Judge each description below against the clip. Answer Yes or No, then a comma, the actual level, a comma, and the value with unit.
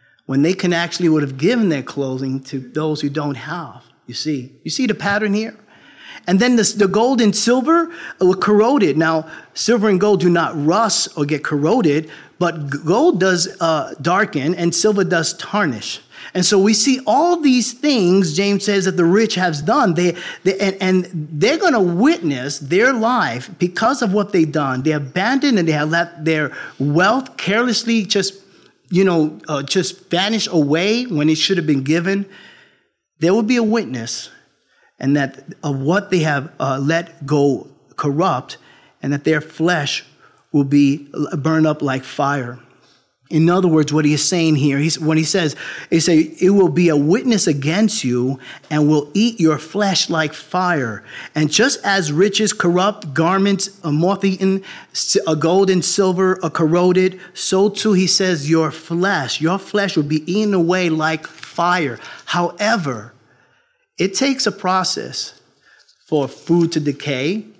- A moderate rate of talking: Yes, average, 170 wpm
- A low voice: No, medium, 175 Hz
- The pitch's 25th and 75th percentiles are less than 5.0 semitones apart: Yes, average, 4.6 semitones